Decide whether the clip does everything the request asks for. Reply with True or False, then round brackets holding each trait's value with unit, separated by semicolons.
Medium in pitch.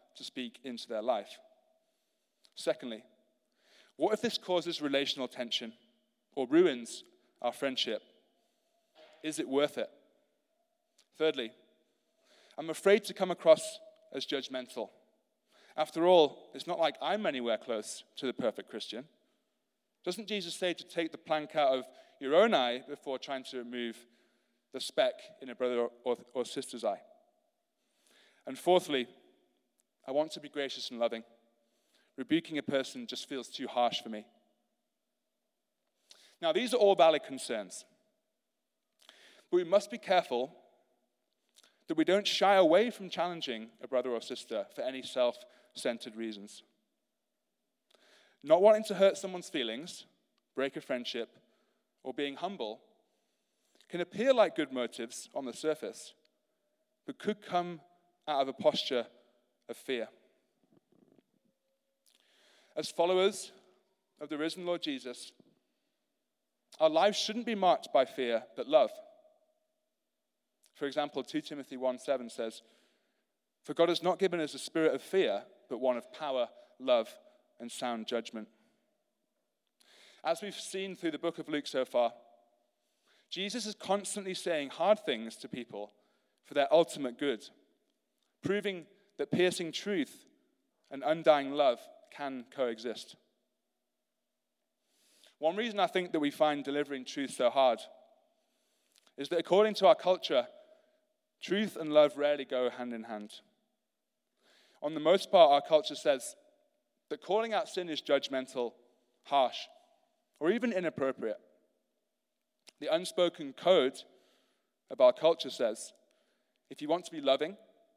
True (175 Hz)